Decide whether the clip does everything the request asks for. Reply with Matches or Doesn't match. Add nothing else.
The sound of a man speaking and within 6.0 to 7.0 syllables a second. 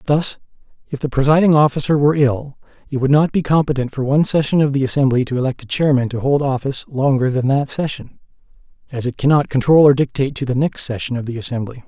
Matches